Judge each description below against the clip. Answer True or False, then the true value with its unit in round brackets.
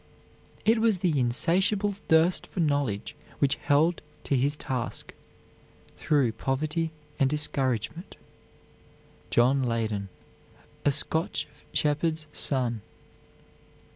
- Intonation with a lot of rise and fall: False (4.5 semitones)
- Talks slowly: True (95 wpm)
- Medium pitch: True (145 Hz)